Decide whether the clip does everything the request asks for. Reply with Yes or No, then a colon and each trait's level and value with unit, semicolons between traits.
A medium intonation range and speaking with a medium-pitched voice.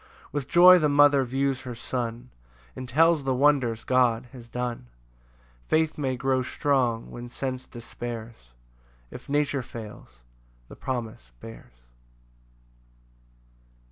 No: average, 3.0 semitones; low, 130 Hz